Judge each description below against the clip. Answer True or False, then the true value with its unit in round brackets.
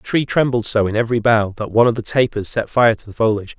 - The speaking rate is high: True (285 wpm)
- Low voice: True (115 Hz)